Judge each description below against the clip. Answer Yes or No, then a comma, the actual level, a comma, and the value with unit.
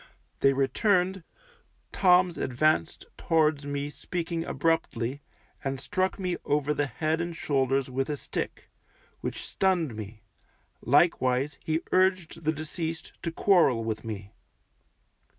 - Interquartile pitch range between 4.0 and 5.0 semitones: Yes, average, 4.3 semitones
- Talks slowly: Yes, slow, 120 wpm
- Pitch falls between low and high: Yes, medium, 155 Hz